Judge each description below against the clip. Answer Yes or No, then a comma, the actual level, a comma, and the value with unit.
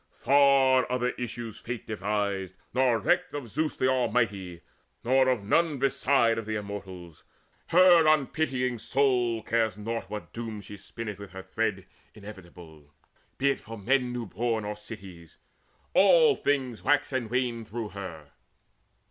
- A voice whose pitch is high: No, low, 115 Hz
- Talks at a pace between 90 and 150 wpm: Yes, average, 145 wpm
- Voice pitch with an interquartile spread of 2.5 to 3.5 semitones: No, average, 4.3 semitones